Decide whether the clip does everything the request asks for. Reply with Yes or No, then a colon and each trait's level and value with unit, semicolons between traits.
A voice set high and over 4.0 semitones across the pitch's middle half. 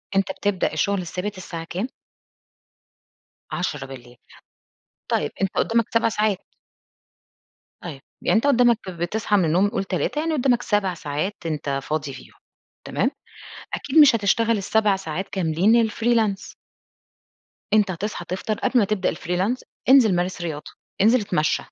Yes: high, 195 Hz; average, 4.5 semitones